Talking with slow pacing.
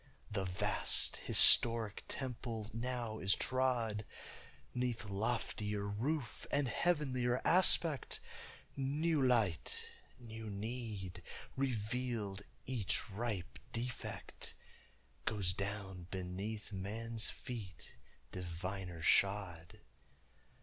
Yes: slow, 80 wpm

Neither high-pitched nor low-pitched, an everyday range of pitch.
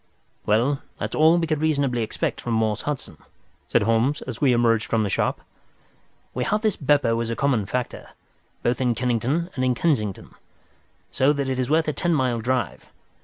No: low, 130 Hz; average, 4.2 semitones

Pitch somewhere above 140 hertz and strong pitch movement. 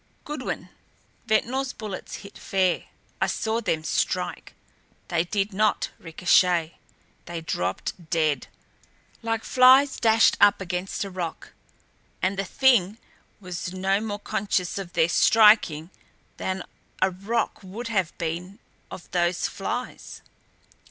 No: high, 190 Hz; average, 3.9 semitones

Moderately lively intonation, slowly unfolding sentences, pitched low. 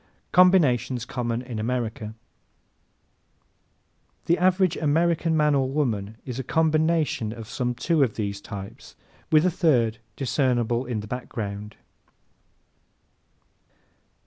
No: wide, 5.7 semitones; slow, 115 wpm; low, 125 Hz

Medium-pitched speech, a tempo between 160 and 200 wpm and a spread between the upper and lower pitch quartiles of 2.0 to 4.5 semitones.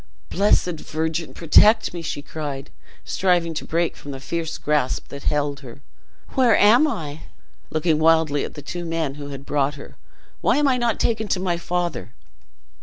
Yes: medium, 160 Hz; average, 175 wpm; average, 3.5 semitones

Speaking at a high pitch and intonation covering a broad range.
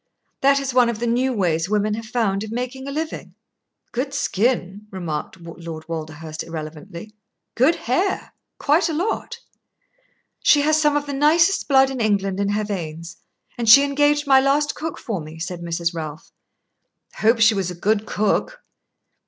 Yes: high, 220 Hz; wide, 8.0 semitones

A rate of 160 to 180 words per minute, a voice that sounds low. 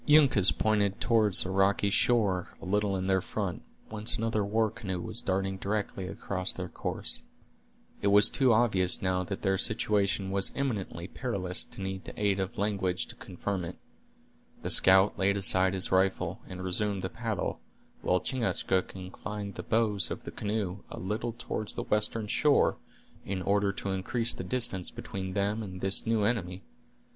Yes: average, 170 wpm; low, 100 Hz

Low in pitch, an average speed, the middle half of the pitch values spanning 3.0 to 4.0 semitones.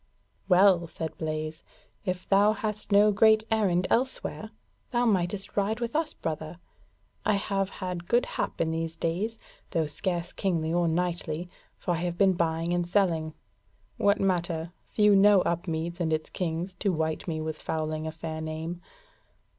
No: medium, 175 Hz; average, 160 wpm; average, 3.6 semitones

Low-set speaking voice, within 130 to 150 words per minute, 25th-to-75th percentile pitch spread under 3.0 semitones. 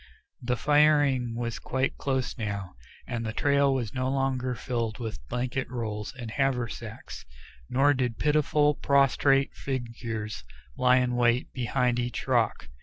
Yes: low, 125 Hz; slow, 135 wpm; narrow, 2.6 semitones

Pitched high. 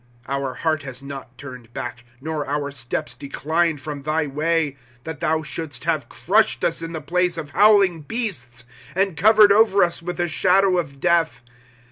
No: medium, 155 Hz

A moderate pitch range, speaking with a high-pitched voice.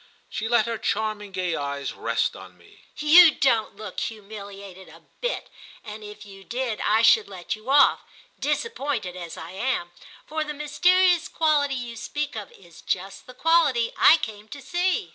No: wide, 7.0 semitones; high, 220 Hz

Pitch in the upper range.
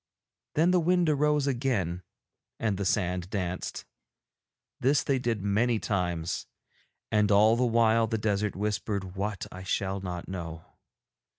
No: low, 105 Hz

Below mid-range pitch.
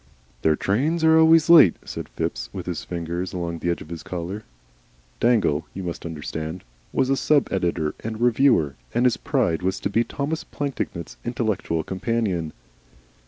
Yes: very low, 95 Hz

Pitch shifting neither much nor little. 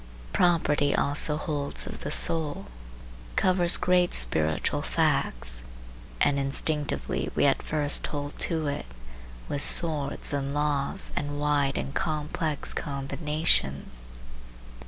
No: narrow, 2.0 semitones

